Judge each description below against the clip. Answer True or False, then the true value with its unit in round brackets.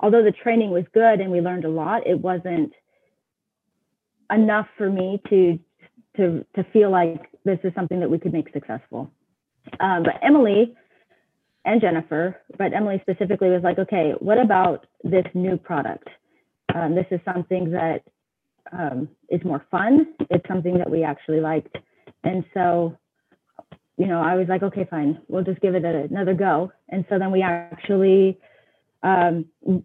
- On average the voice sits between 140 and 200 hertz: True (185 Hz)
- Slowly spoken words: False (165 wpm)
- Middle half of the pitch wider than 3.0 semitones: False (2.4 semitones)